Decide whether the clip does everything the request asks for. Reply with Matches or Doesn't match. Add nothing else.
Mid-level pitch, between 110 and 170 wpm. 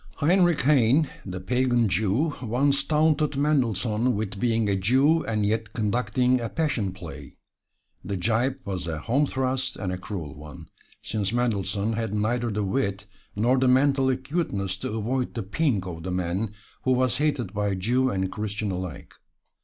Doesn't match